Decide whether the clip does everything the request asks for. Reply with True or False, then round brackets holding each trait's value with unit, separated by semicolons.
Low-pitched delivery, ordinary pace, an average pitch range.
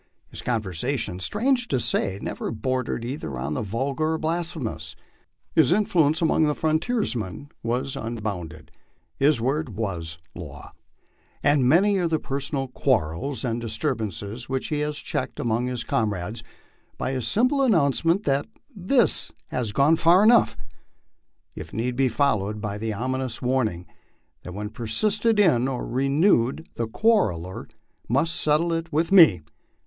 False (130 Hz; 145 wpm; 6.5 semitones)